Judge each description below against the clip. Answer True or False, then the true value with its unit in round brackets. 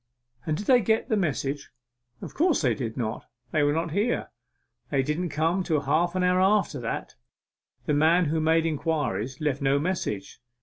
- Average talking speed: True (180 wpm)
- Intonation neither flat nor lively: True (4.4 semitones)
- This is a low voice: False (155 Hz)